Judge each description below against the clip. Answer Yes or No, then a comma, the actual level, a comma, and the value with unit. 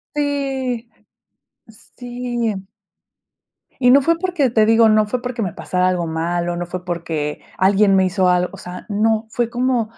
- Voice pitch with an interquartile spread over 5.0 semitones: Yes, wide, 5.4 semitones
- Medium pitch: No, high, 220 Hz